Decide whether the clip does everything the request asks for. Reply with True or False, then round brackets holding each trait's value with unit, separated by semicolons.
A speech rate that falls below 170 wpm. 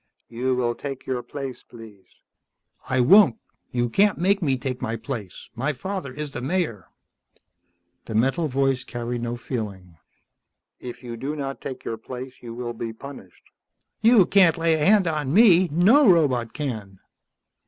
True (160 wpm)